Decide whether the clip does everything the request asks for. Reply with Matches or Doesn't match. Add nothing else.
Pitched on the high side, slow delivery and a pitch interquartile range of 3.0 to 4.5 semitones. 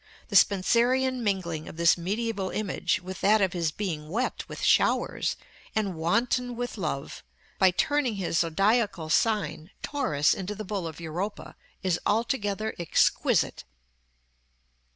Doesn't match